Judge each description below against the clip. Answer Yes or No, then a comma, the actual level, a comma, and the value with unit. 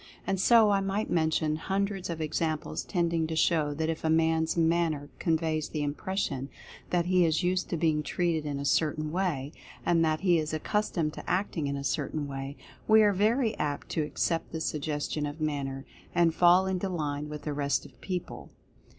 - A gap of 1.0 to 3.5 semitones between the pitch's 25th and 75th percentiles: Yes, average, 3.1 semitones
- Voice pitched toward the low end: No, medium, 160 Hz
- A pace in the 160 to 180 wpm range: No, average, 195 wpm